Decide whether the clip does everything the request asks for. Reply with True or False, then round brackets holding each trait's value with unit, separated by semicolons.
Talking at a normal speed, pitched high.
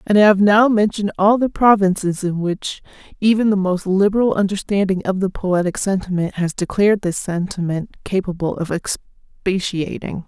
True (150 wpm; 195 Hz)